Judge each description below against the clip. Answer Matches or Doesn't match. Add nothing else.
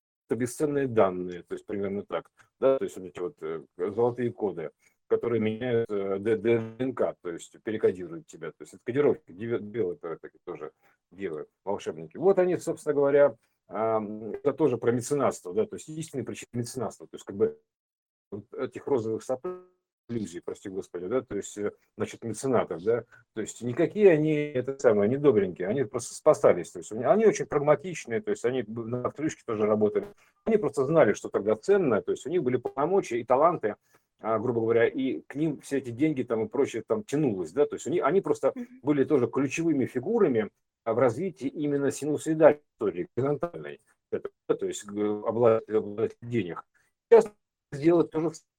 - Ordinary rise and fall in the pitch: Doesn't match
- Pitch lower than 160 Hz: Matches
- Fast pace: Matches